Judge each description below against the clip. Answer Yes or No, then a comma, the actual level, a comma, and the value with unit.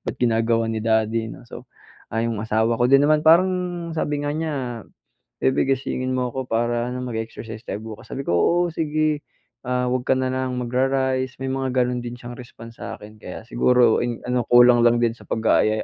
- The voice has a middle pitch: No, low, 125 Hz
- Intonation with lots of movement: No, narrow, 2.5 semitones